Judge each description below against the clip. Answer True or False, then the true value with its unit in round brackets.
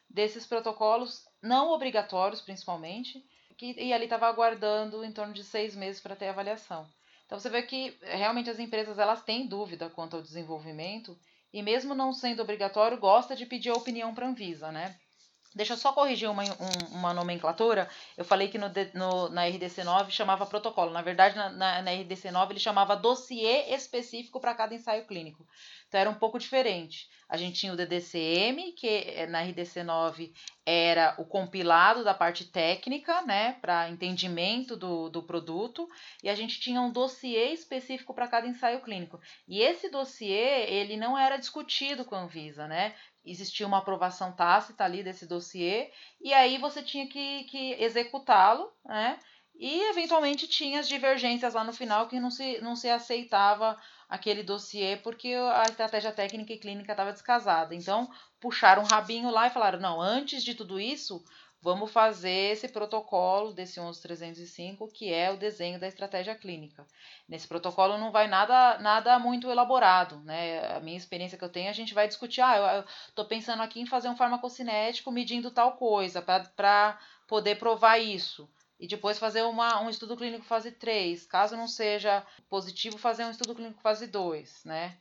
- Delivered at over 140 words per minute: True (170 wpm)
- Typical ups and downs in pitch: True (4.7 semitones)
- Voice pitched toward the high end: True (210 Hz)